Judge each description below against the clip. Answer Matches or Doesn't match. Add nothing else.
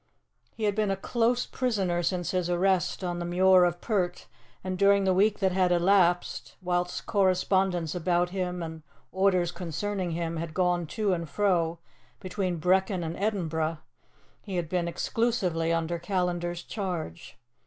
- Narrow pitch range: Matches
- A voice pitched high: Doesn't match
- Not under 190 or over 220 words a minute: Doesn't match